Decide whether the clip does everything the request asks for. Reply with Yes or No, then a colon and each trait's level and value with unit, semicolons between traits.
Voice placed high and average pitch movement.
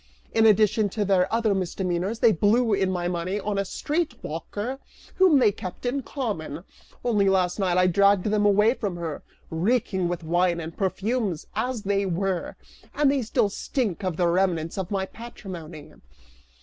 Yes: high, 195 Hz; average, 3.8 semitones